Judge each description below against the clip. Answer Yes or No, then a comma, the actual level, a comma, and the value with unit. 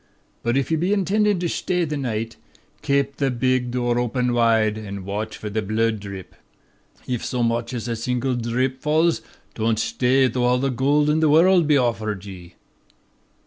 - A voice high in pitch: No, low, 125 Hz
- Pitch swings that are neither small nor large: Yes, average, 3.9 semitones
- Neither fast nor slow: Yes, average, 185 wpm